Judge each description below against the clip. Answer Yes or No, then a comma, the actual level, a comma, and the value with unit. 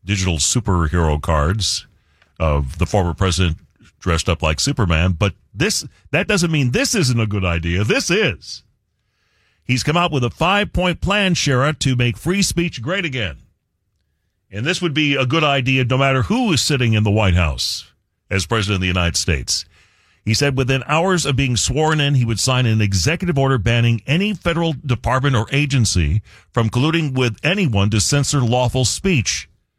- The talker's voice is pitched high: No, low, 120 Hz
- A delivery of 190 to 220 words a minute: No, average, 175 wpm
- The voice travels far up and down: Yes, wide, 7.4 semitones